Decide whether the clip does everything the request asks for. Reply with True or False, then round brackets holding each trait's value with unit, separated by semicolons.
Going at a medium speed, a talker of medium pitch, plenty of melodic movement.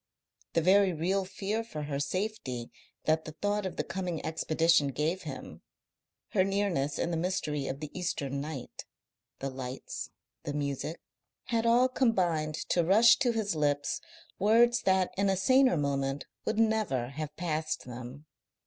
True (155 wpm; 165 Hz; 5.8 semitones)